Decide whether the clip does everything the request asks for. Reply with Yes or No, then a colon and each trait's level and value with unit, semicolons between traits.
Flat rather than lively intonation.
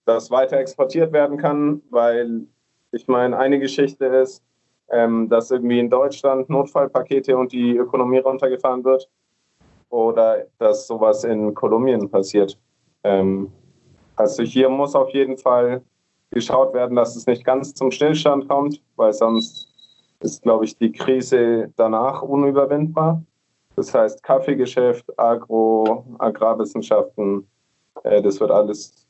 No: average, 3.3 semitones